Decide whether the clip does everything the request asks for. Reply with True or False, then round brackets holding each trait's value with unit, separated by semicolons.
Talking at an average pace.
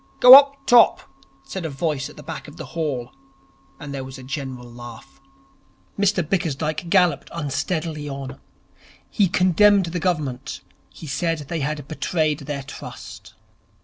True (145 wpm)